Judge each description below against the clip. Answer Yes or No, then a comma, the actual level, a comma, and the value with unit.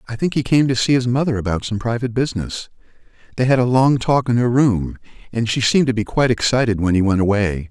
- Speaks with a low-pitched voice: Yes, low, 115 Hz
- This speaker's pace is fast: Yes, fast, 240 wpm